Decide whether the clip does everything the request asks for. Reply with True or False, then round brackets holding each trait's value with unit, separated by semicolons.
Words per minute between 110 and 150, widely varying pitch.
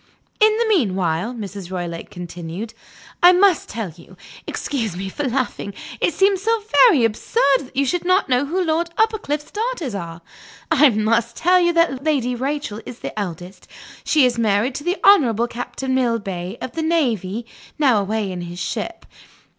False (170 wpm; 8.4 semitones)